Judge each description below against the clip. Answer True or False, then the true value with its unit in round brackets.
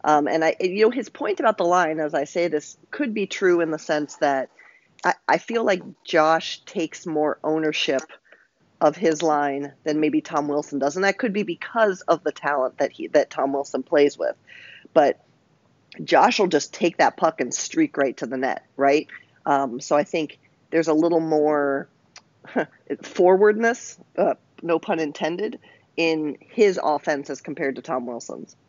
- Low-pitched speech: False (160 Hz)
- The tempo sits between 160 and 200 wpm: True (185 wpm)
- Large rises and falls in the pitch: False (3.9 semitones)